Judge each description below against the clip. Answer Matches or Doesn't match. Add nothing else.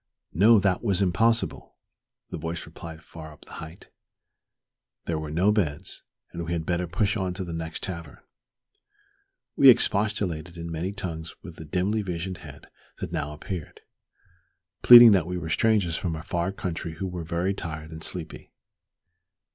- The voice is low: Matches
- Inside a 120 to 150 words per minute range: Doesn't match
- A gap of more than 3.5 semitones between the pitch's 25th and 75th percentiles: Doesn't match